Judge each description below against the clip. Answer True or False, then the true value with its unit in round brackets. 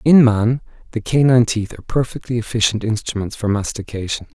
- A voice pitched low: True (115 Hz)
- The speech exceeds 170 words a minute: False (150 wpm)